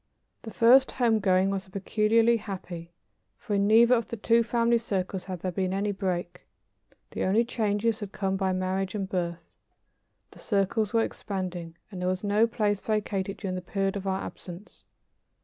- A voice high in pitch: Yes, high, 195 Hz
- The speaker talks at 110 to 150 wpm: No, average, 175 wpm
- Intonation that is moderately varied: Yes, average, 3.0 semitones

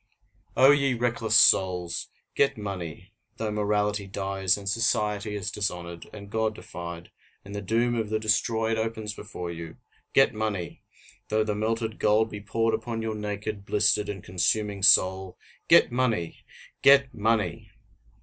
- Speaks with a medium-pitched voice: No, low, 105 Hz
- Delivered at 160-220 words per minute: No, average, 145 wpm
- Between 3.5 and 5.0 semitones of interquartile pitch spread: No, narrow, 2.4 semitones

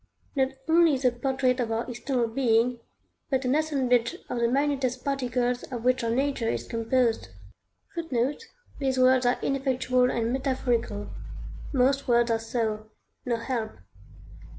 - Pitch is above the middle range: Yes, very high, 250 Hz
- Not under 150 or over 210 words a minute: No, slow, 135 wpm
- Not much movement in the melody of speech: Yes, narrow, 2.3 semitones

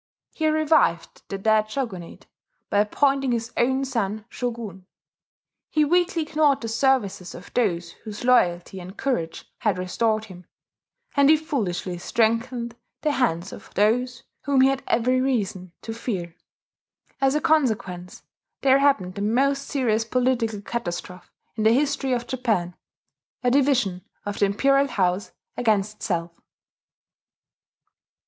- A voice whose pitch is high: Yes, high, 230 Hz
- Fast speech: No, slow, 135 wpm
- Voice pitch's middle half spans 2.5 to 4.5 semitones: No, wide, 5.5 semitones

